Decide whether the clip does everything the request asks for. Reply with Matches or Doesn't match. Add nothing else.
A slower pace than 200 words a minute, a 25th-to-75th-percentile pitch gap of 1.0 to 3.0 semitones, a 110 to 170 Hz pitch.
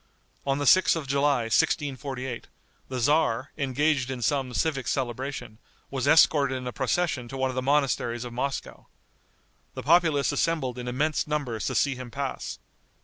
Matches